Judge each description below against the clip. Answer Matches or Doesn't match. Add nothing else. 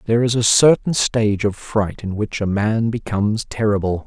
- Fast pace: Doesn't match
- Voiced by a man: Matches